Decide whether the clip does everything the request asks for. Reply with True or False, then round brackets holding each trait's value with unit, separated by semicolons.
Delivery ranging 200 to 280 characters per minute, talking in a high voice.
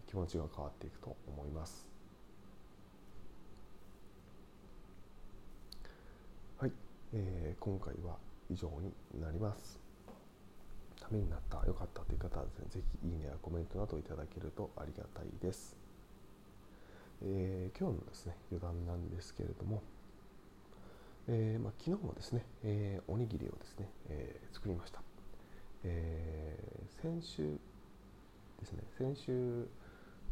False (250 characters per minute; 95 Hz)